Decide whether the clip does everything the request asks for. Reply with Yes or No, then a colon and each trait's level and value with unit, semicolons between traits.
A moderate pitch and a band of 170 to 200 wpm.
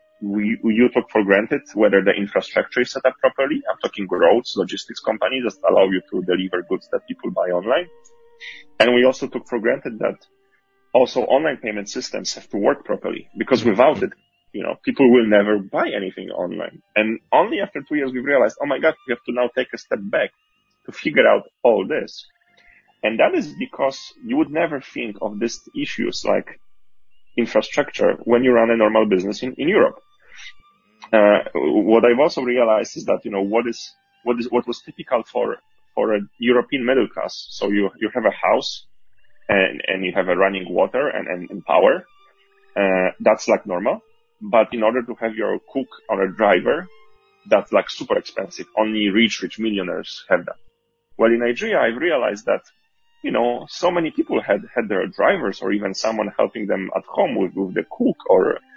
No: low, 125 Hz; average, 195 wpm